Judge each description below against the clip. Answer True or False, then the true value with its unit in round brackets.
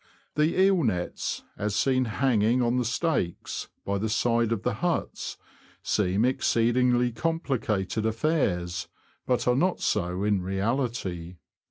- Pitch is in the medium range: False (115 Hz)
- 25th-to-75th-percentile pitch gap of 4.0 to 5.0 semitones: True (4.4 semitones)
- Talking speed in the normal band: False (130 wpm)